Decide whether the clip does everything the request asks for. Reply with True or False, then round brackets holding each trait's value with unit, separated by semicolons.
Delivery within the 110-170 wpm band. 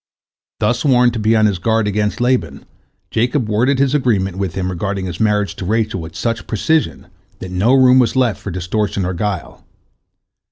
False (185 wpm)